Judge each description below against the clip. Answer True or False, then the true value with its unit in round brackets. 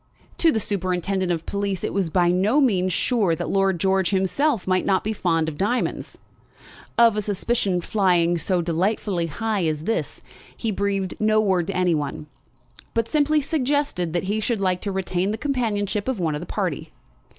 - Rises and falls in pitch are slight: False (3.5 semitones)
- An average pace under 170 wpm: False (185 wpm)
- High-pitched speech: True (195 Hz)